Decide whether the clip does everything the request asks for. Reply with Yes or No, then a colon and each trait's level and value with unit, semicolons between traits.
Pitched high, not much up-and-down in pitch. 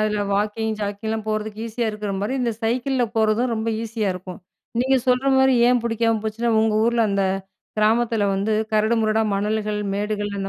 Yes: high, 220 Hz; narrow, 1.9 semitones